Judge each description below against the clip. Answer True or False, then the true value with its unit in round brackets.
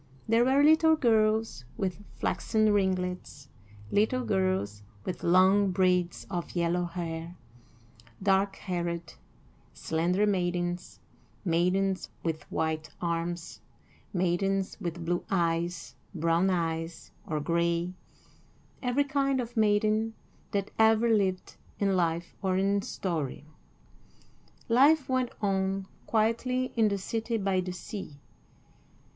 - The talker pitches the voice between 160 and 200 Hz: True (190 Hz)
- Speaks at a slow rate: True (110 wpm)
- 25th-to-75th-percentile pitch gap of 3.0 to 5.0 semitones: True (3.9 semitones)